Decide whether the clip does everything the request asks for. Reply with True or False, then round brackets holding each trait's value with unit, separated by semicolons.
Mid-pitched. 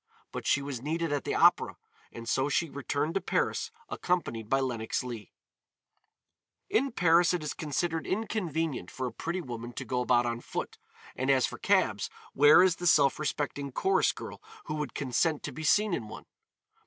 True (145 Hz)